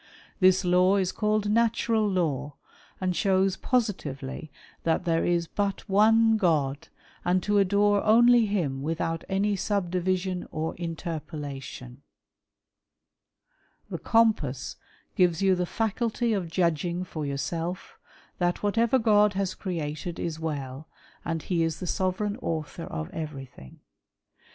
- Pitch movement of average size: Yes, average, 4.3 semitones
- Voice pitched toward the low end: No, medium, 180 Hz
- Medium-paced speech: No, slow, 130 wpm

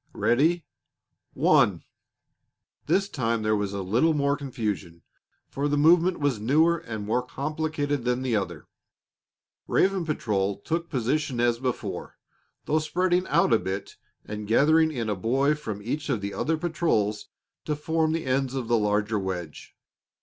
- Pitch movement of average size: No, wide, 6.6 semitones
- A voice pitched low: Yes, low, 130 Hz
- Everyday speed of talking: Yes, average, 150 wpm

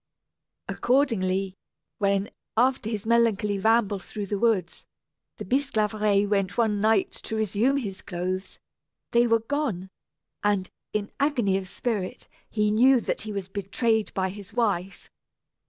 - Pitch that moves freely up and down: No, average, 2.9 semitones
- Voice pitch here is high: Yes, high, 210 Hz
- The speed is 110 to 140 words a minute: Yes, slow, 135 wpm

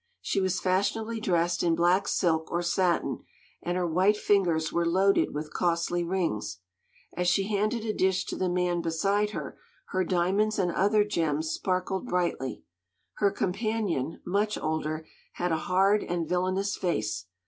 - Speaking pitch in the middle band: Yes, medium, 180 Hz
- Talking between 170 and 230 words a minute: No, average, 155 wpm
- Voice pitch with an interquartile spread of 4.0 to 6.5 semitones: No, average, 2.9 semitones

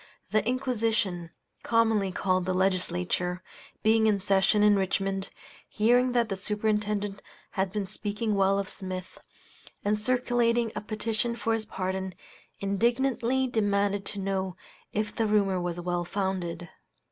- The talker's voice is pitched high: Yes, high, 205 Hz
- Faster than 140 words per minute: No, slow, 135 wpm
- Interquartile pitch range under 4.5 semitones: Yes, average, 2.8 semitones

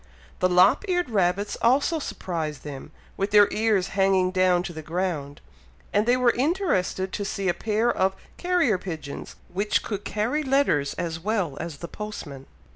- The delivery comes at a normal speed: Yes, average, 165 wpm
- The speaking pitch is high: Yes, high, 195 Hz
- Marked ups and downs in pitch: No, average, 4.4 semitones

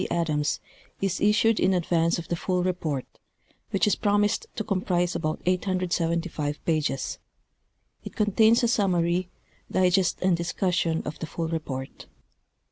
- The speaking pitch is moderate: Yes, medium, 180 Hz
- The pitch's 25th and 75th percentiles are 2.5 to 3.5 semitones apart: Yes, average, 2.9 semitones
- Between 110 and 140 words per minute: Yes, slow, 135 wpm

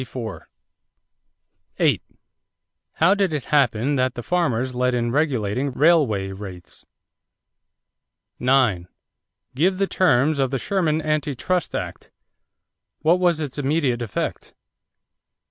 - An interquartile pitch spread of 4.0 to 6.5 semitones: Yes, average, 4.7 semitones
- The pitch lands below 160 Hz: Yes, low, 135 Hz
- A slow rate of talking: Yes, slow, 105 wpm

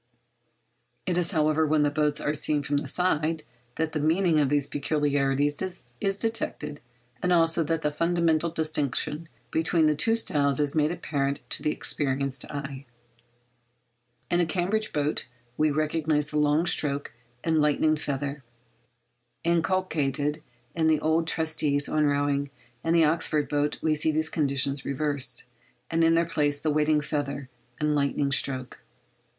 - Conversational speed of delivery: Yes, average, 150 wpm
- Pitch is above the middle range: No, medium, 150 Hz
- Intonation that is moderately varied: No, narrow, 2.1 semitones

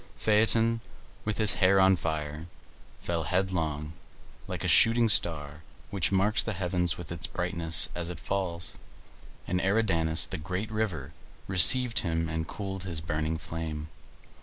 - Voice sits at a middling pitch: No, very low, 90 Hz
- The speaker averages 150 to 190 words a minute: No, average, 140 wpm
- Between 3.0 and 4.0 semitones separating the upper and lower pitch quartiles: Yes, average, 3.3 semitones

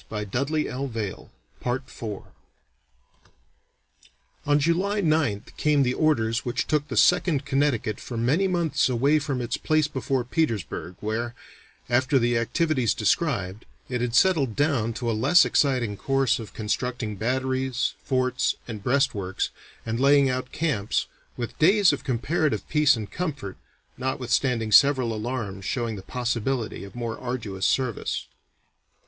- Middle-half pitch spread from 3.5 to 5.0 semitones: Yes, average, 4.0 semitones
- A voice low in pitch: Yes, low, 125 Hz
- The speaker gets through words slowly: Yes, slow, 130 wpm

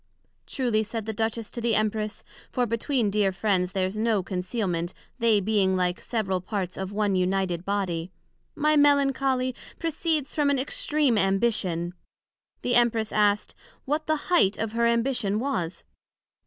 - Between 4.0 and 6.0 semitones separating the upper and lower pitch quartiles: Yes, average, 4.5 semitones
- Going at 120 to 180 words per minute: Yes, average, 145 wpm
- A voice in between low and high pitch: No, high, 215 Hz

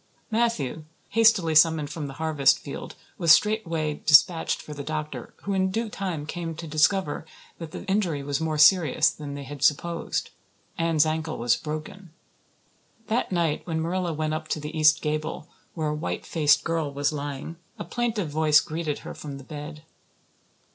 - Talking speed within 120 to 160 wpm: No, average, 170 wpm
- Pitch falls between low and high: Yes, medium, 155 Hz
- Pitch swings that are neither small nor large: No, narrow, 2.2 semitones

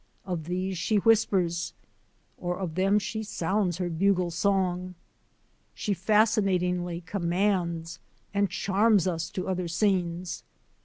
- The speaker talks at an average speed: No, slow, 120 wpm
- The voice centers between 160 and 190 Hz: Yes, medium, 185 Hz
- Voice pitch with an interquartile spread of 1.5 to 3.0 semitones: Yes, narrow, 2.5 semitones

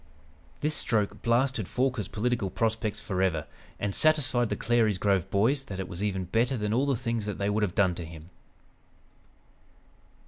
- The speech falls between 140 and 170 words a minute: Yes, average, 165 wpm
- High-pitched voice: No, low, 105 Hz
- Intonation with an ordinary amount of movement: Yes, average, 4.0 semitones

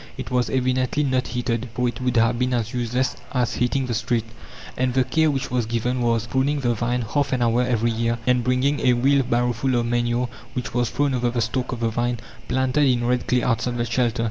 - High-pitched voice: No, low, 125 Hz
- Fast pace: Yes, fast, 225 wpm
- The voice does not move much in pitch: Yes, narrow, 1.3 semitones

